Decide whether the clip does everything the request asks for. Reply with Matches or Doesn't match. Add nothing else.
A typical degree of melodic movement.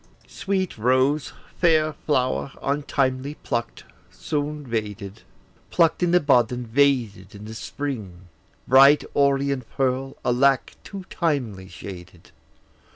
Matches